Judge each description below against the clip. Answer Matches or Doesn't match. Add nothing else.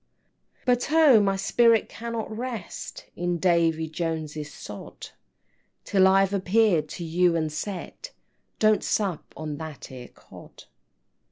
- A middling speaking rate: Doesn't match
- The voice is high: Doesn't match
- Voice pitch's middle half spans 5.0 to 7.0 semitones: Matches